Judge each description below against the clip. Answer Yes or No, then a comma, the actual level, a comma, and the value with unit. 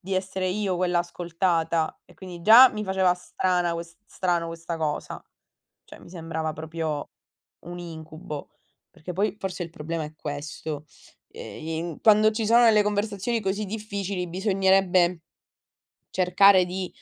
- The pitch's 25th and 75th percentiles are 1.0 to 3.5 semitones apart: Yes, average, 2.8 semitones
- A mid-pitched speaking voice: Yes, medium, 180 Hz